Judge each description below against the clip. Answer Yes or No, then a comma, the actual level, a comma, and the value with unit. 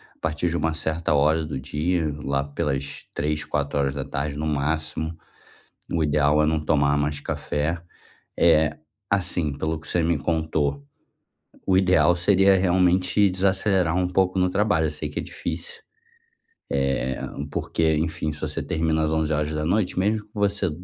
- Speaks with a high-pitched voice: No, very low, 80 Hz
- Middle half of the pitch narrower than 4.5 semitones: Yes, average, 3.3 semitones